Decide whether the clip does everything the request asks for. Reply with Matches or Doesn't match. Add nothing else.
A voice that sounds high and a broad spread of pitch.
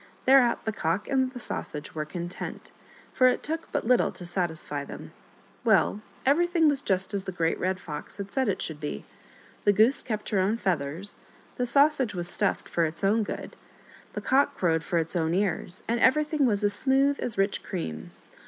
Matches